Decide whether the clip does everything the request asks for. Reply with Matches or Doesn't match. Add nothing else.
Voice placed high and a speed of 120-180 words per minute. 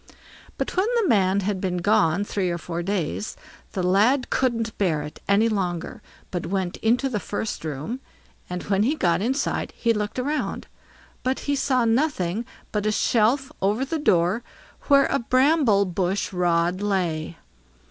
Matches